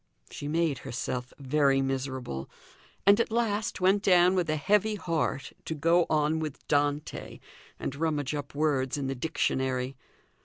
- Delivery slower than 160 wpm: Yes, average, 150 wpm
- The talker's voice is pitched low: No, medium, 150 Hz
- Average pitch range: Yes, average, 4.3 semitones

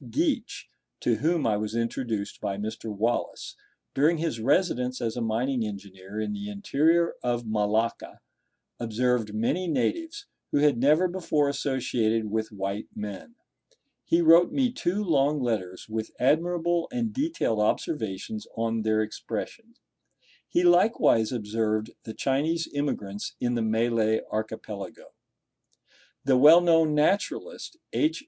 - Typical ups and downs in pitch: No, wide, 7.3 semitones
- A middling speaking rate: No, slow, 130 wpm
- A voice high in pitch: No, low, 125 Hz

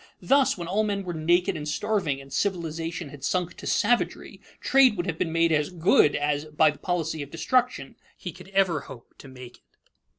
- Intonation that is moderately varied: Yes, average, 4.3 semitones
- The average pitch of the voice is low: No, medium, 165 Hz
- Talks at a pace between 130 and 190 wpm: No, average, 200 wpm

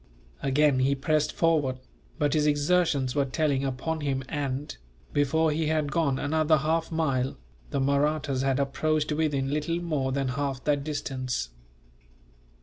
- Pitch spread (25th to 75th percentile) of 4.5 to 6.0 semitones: No, narrow, 2.4 semitones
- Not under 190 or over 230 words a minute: No, average, 145 wpm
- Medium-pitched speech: Yes, medium, 145 Hz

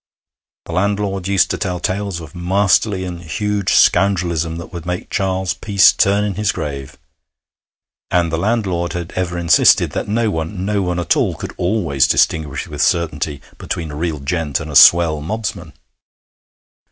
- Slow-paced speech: No, average, 165 wpm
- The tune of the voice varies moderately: Yes, average, 3.4 semitones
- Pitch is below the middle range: Yes, very low, 90 Hz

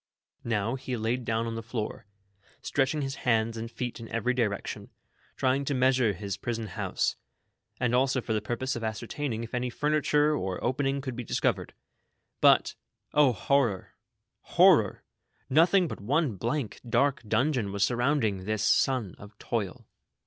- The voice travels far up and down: No, average, 3.4 semitones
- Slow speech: No, average, 155 wpm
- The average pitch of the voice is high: No, low, 120 Hz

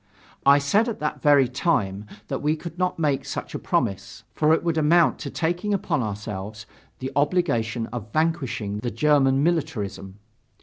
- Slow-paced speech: No, average, 165 wpm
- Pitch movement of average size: No, wide, 6.5 semitones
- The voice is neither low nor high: Yes, medium, 145 Hz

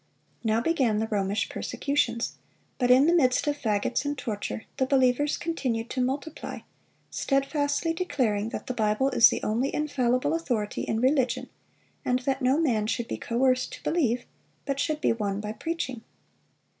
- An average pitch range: Yes, average, 4.1 semitones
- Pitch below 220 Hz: No, very high, 255 Hz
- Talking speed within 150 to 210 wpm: Yes, average, 160 wpm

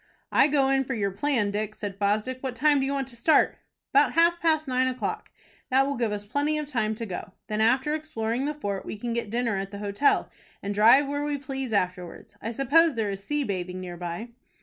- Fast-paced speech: Yes, fast, 230 wpm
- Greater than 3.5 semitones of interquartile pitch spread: Yes, wide, 5.5 semitones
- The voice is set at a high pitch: Yes, high, 240 Hz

